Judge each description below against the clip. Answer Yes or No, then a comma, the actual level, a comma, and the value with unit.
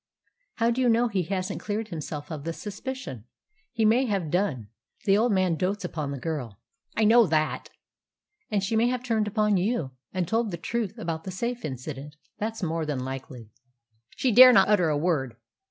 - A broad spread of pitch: Yes, wide, 6.4 semitones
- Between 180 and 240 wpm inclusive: Yes, average, 195 wpm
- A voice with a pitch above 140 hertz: Yes, high, 190 Hz